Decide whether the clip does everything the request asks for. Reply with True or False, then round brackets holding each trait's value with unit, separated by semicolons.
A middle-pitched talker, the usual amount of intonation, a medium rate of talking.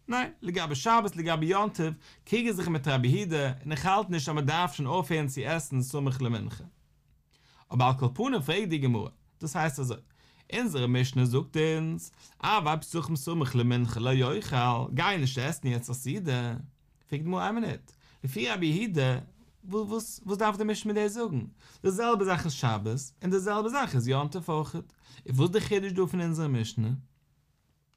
False (155 Hz; 6.5 semitones; 170 wpm)